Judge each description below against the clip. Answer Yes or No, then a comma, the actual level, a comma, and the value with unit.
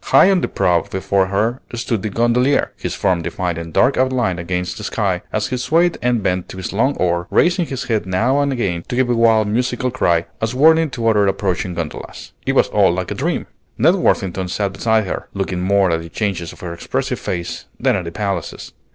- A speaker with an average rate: No, fast, 220 wpm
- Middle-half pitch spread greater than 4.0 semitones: Yes, wide, 5.5 semitones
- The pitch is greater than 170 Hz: No, low, 105 Hz